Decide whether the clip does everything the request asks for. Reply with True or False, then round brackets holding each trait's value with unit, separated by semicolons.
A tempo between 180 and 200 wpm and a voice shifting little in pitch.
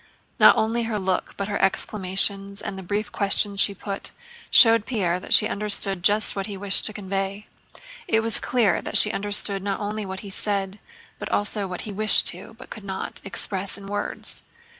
True (190 wpm; 1.5 semitones)